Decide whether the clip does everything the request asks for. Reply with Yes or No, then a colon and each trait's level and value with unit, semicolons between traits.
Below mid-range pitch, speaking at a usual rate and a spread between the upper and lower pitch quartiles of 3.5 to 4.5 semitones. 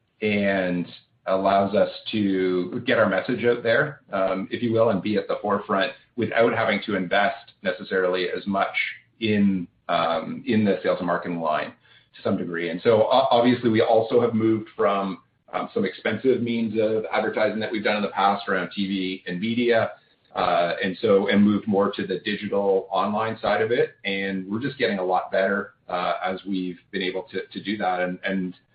No: low, 100 Hz; average, 190 wpm; average, 2.8 semitones